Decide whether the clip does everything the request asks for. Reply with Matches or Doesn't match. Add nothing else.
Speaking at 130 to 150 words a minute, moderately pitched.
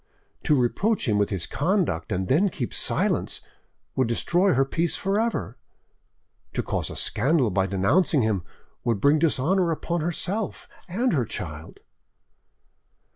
Matches